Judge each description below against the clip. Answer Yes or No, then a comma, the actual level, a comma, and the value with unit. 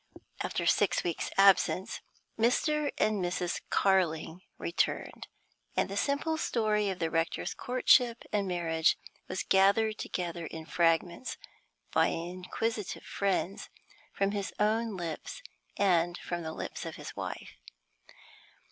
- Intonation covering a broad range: No, average, 3.9 semitones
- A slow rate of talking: Yes, slow, 120 wpm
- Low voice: No, high, 190 Hz